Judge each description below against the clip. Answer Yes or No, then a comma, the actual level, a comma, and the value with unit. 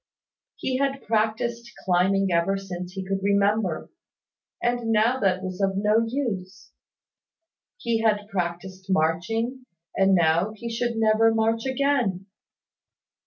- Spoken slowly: Yes, slow, 120 wpm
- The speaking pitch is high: Yes, high, 210 Hz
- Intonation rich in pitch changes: No, average, 3.4 semitones